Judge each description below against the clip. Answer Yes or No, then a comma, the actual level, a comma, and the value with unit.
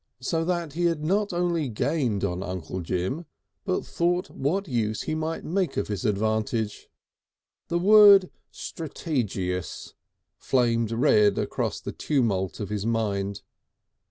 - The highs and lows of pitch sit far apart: Yes, wide, 8.6 semitones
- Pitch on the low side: Yes, low, 125 Hz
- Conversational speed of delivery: No, slow, 130 wpm